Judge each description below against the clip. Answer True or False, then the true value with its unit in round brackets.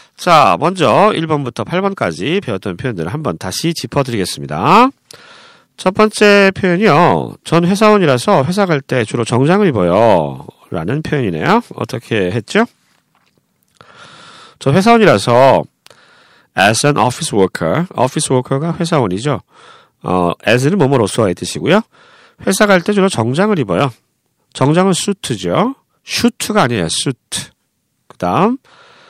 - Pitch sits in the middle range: True (175 Hz)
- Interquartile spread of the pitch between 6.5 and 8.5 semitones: True (8.0 semitones)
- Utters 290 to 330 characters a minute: True (310 characters per minute)